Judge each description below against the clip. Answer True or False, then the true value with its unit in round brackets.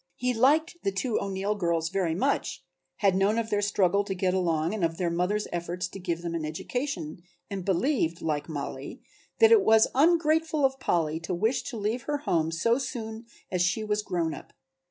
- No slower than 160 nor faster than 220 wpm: True (195 wpm)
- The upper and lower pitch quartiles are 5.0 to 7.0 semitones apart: True (5.6 semitones)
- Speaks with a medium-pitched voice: False (195 Hz)